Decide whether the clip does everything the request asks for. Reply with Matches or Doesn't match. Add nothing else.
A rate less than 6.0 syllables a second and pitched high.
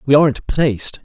Doesn't match